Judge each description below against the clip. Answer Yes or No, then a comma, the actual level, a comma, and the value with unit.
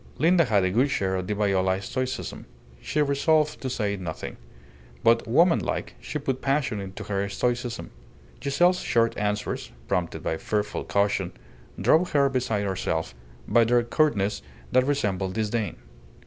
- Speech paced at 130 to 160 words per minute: Yes, average, 150 wpm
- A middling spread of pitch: No, wide, 5.8 semitones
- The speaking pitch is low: Yes, low, 115 Hz